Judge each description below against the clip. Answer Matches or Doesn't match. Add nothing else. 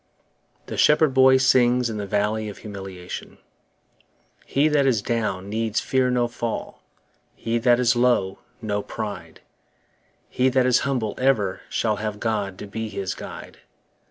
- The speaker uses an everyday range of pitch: Matches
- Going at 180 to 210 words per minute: Doesn't match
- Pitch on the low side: Matches